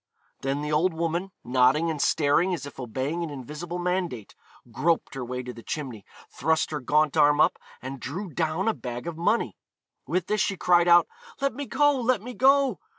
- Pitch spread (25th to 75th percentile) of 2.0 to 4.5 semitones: No, average, 4.9 semitones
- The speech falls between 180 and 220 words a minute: Yes, average, 195 wpm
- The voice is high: No, medium, 160 Hz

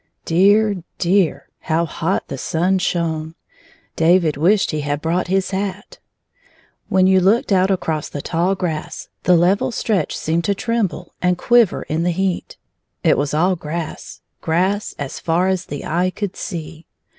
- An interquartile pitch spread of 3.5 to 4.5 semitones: No, average, 2.9 semitones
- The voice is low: No, medium, 180 Hz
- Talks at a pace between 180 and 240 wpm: No, average, 165 wpm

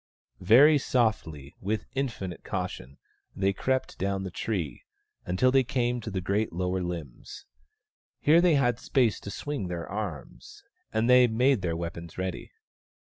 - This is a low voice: Yes, low, 105 Hz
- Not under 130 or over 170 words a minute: Yes, average, 145 wpm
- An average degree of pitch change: No, wide, 6.1 semitones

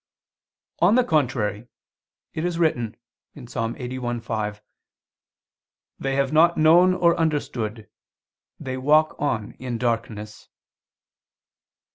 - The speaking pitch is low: Yes, low, 130 Hz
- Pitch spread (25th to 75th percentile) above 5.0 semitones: Yes, wide, 5.6 semitones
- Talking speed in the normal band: No, slow, 95 wpm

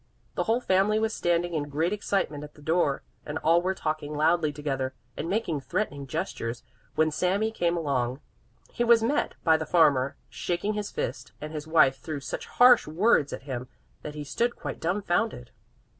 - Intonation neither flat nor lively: Yes, average, 5.0 semitones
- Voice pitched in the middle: Yes, medium, 160 Hz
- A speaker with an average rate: Yes, average, 180 wpm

